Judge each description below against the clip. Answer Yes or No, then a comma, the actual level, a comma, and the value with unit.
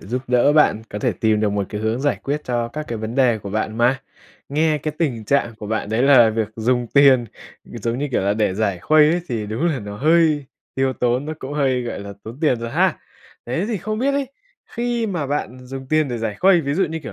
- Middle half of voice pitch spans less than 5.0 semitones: No, average, 5.3 semitones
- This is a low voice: Yes, low, 125 Hz